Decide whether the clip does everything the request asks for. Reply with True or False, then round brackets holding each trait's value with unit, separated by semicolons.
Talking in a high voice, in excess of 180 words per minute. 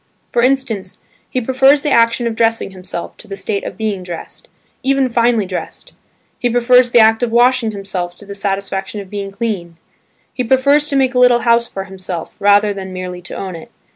True (220 Hz; 200 wpm)